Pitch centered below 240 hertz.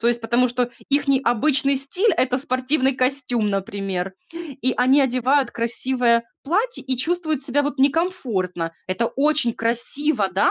No: very high, 255 Hz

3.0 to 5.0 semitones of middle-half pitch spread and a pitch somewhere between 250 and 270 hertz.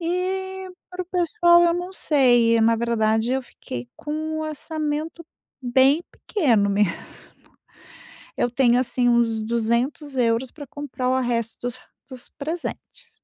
No: wide, 5.6 semitones; very high, 260 Hz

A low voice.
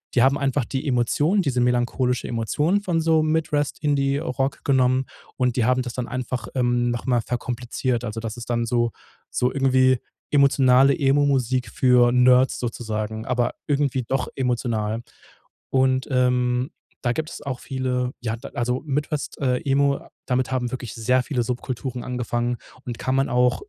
Yes: low, 125 Hz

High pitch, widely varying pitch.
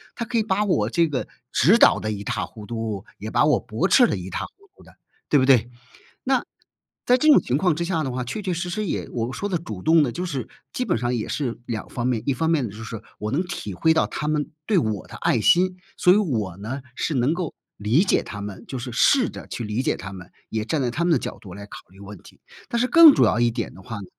No: low, 130 Hz; wide, 8.3 semitones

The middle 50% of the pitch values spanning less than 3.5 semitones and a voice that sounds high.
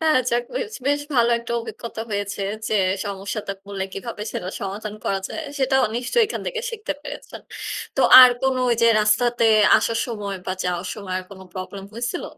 No: average, 4.4 semitones; high, 225 Hz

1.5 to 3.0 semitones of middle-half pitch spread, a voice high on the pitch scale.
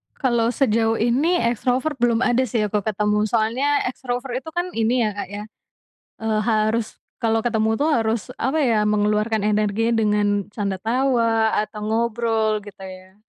Yes: narrow, 2.4 semitones; high, 225 Hz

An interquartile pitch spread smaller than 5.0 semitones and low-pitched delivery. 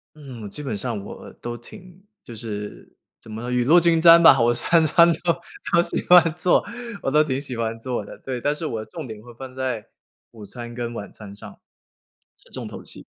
No: wide, 5.6 semitones; low, 125 Hz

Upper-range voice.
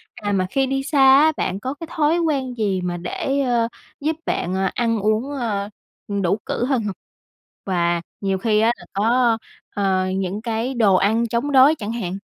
Yes: high, 225 Hz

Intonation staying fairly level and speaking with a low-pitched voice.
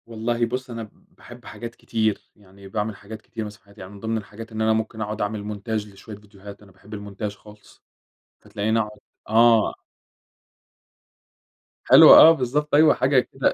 Yes: narrow, 1.9 semitones; low, 110 Hz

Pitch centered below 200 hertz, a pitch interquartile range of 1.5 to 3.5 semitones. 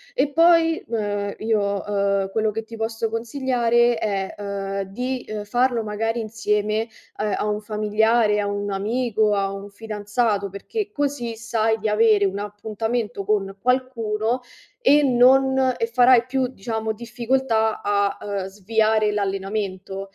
No: high, 220 Hz; average, 2.8 semitones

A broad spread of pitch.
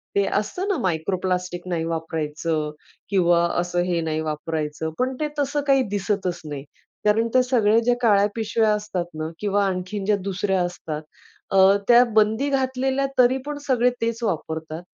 Yes: wide, 5.8 semitones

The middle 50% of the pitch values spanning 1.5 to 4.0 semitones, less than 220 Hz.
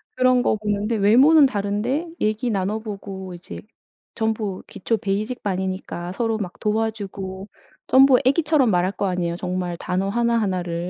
Yes: average, 3.7 semitones; high, 205 Hz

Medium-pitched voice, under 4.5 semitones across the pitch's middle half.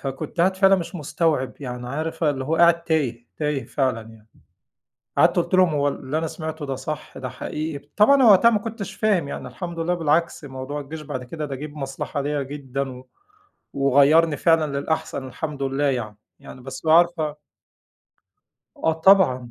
Yes: medium, 150 Hz; average, 3.5 semitones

